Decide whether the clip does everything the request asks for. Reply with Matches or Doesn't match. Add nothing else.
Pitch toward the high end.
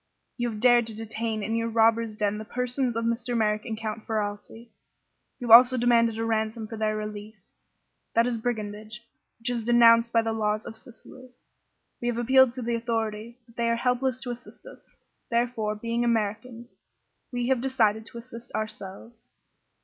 Matches